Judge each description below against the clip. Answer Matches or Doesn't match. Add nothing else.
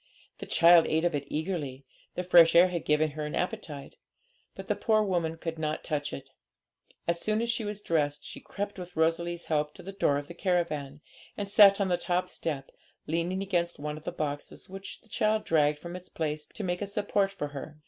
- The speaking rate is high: Matches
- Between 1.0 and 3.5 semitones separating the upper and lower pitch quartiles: Doesn't match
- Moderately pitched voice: Matches